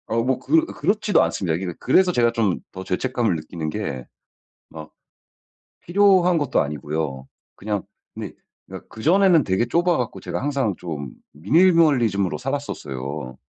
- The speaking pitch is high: No, low, 110 Hz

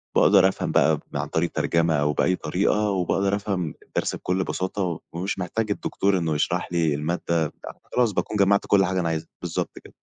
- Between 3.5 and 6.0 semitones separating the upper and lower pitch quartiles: No, average, 3.1 semitones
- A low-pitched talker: Yes, very low, 90 Hz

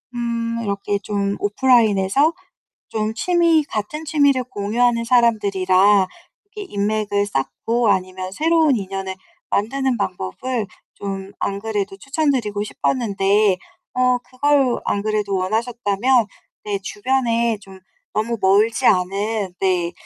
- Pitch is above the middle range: Yes, high, 215 Hz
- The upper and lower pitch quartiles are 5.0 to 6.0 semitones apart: No, average, 3.9 semitones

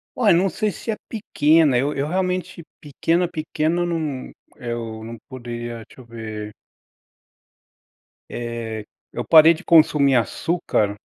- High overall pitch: No, medium, 145 Hz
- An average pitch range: No, wide, 6.3 semitones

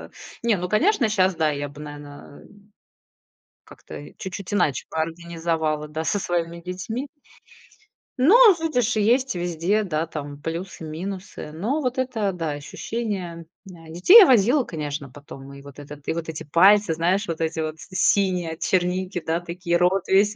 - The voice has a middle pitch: Yes, medium, 175 Hz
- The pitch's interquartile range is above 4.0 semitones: Yes, average, 4.4 semitones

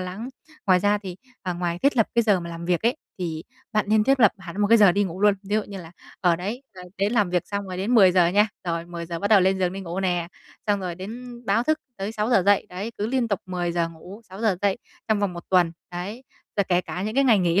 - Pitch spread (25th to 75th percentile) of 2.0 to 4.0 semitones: Yes, average, 3.1 semitones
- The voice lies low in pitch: No, high, 195 Hz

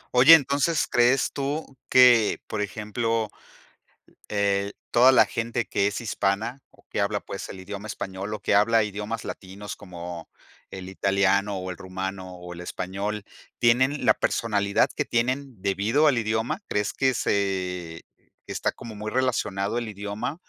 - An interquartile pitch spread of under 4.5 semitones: Yes, average, 3.5 semitones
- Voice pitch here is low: Yes, low, 105 Hz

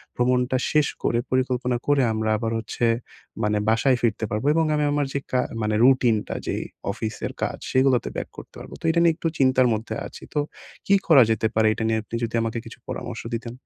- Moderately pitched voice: No, low, 120 Hz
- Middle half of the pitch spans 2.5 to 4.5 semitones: Yes, average, 3.0 semitones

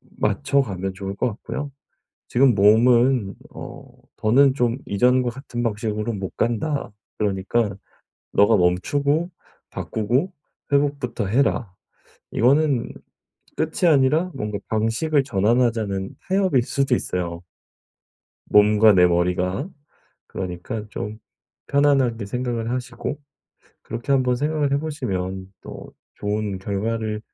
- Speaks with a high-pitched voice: No, low, 115 Hz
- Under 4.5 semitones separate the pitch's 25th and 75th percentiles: No, average, 5.1 semitones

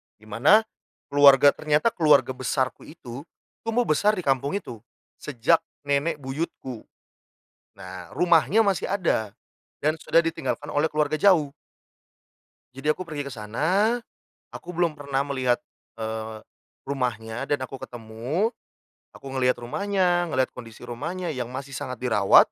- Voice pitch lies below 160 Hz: Yes, medium, 140 Hz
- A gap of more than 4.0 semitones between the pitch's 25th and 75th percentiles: Yes, average, 5.2 semitones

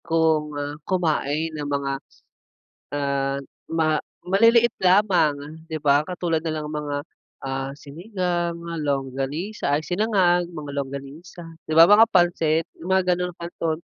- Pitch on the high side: No, medium, 160 Hz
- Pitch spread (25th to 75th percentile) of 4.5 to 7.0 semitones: No, average, 3.8 semitones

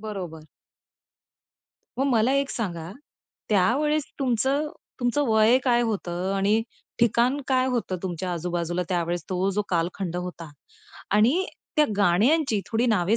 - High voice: Yes, high, 215 Hz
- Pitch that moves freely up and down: Yes, wide, 5.8 semitones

